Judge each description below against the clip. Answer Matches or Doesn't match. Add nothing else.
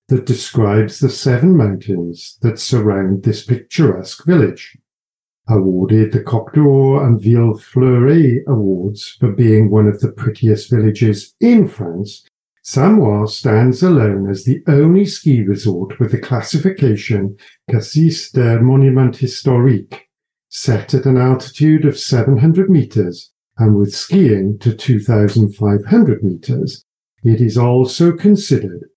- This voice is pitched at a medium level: Doesn't match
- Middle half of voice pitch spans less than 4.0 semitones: Doesn't match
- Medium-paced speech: Doesn't match